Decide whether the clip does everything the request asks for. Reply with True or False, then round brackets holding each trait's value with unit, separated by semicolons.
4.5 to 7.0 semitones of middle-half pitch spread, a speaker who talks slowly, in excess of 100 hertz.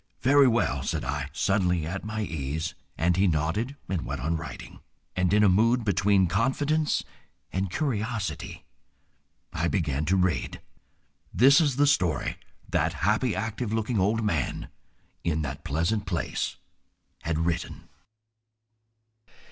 False (5.4 semitones; 130 wpm; 95 Hz)